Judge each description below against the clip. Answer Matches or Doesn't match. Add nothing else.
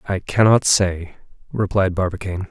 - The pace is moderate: Doesn't match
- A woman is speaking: Doesn't match